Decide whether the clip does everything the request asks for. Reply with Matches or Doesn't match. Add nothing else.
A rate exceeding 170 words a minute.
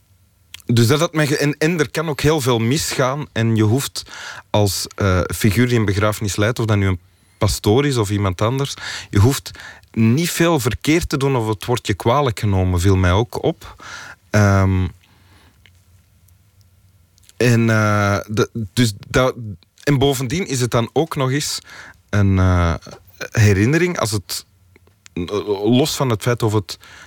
Doesn't match